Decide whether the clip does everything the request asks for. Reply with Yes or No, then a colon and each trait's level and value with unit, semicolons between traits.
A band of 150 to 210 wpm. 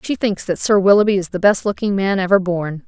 No: fast, 250 wpm